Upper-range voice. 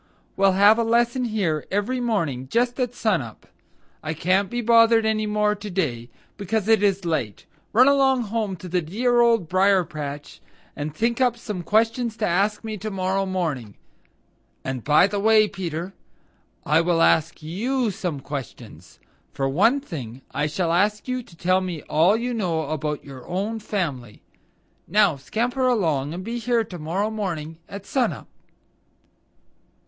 Yes: high, 195 Hz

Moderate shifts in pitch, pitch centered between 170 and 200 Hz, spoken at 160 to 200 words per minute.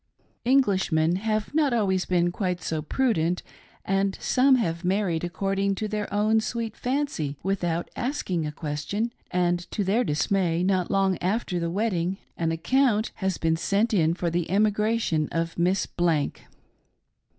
No: average, 4.1 semitones; high, 190 Hz; average, 150 wpm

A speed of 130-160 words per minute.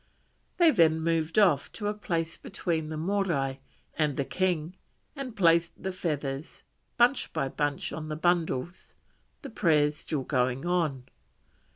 Yes: average, 145 wpm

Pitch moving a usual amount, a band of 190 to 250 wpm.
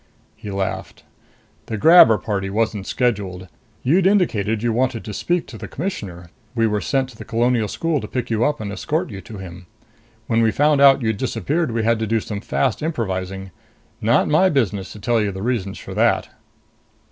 Yes: average, 4.6 semitones; average, 195 wpm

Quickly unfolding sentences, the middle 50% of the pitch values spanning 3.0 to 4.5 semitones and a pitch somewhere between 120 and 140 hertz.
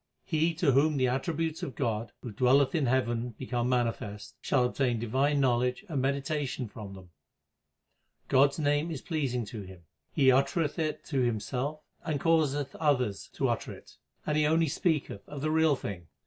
No: average, 175 wpm; average, 4.0 semitones; low, 135 Hz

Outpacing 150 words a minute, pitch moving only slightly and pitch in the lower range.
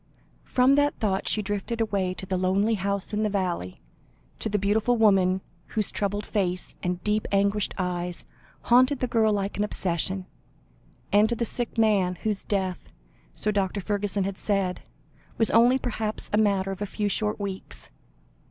No: average, 170 wpm; narrow, 2.3 semitones; high, 205 Hz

